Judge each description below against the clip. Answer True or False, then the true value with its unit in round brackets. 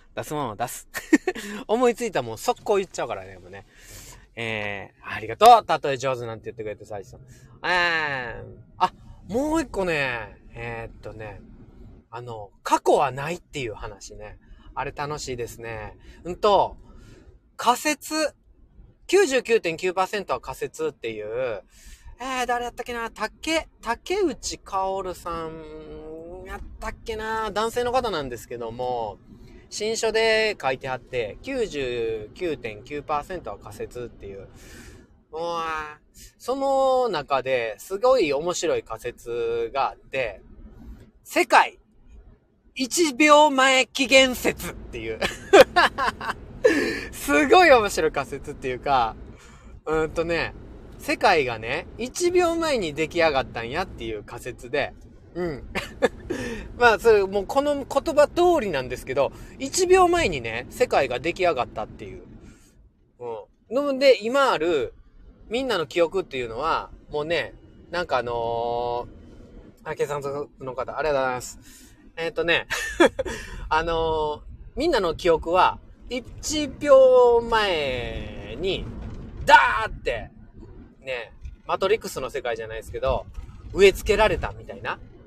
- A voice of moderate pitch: True (170 Hz)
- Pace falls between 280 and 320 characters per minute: False (245 characters per minute)